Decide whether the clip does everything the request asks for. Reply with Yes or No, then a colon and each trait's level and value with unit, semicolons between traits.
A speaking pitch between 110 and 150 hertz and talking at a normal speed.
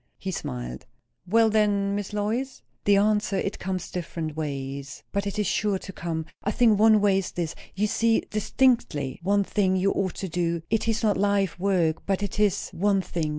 No: high, 195 Hz; average, 195 wpm